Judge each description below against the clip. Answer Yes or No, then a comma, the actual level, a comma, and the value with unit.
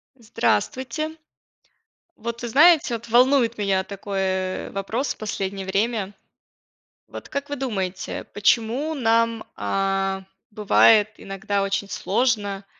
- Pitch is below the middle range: No, high, 215 Hz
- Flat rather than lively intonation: No, average, 3.6 semitones